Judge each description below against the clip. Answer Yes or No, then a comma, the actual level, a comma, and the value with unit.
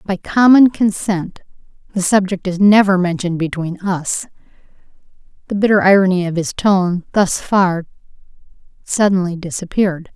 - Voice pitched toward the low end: No, medium, 185 Hz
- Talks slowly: Yes, slow, 120 wpm